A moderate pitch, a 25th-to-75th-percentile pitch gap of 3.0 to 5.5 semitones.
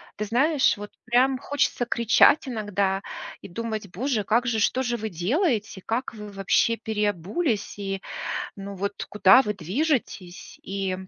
No: high, 215 Hz; average, 3.7 semitones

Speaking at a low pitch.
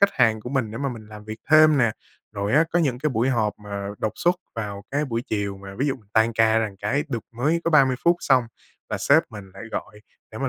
Yes: low, 115 Hz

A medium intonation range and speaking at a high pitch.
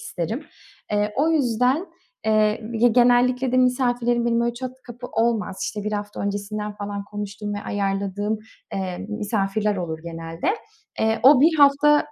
Yes: average, 3.3 semitones; high, 220 Hz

